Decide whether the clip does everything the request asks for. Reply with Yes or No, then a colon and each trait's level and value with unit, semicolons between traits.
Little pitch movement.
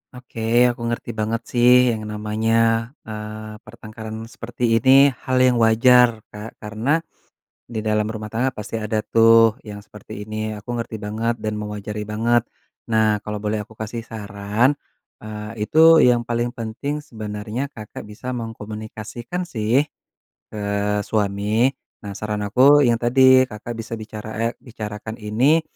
Yes: narrow, 2.0 semitones